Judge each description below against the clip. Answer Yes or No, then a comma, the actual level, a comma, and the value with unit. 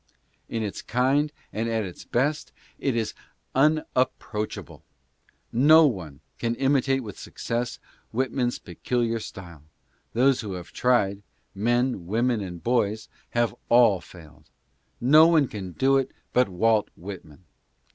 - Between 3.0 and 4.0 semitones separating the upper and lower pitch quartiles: No, average, 4.8 semitones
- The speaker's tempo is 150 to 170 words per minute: No, average, 140 wpm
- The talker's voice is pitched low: Yes, low, 115 Hz